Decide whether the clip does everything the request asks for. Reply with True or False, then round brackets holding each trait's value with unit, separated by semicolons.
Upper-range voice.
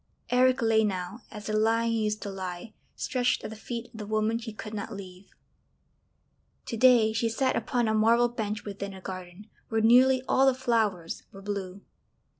True (220 Hz)